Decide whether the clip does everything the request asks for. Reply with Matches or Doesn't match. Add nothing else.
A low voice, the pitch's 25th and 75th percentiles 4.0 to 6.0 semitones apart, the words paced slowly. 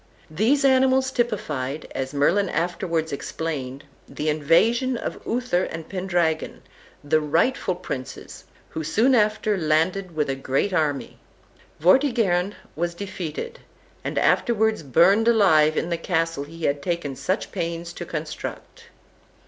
Doesn't match